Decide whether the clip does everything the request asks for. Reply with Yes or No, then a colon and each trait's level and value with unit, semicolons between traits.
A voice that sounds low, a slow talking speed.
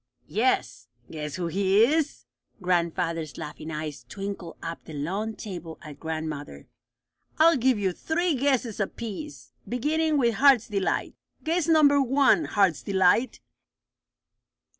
No: high, 205 Hz; slow, 120 wpm